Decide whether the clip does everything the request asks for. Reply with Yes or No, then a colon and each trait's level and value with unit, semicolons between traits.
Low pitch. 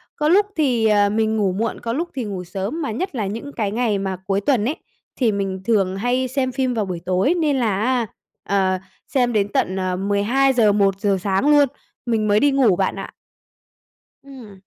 No: high, 220 Hz